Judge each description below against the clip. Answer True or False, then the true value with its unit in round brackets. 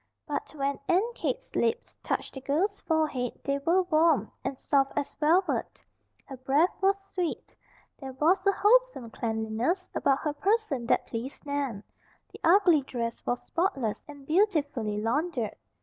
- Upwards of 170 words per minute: False (150 wpm)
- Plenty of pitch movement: True (5.9 semitones)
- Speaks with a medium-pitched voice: False (295 Hz)